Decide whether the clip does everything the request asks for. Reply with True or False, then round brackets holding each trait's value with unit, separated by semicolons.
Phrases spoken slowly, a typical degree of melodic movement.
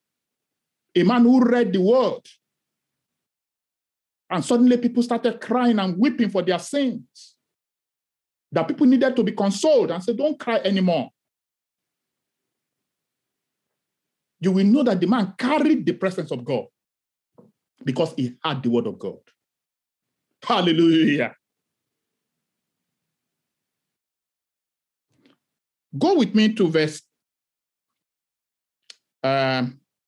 False (105 wpm; 6.8 semitones)